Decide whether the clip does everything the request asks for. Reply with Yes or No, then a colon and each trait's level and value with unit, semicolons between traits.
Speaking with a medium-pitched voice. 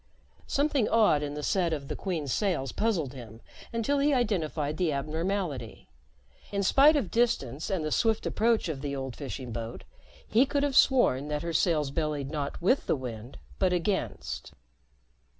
Yes: medium, 160 Hz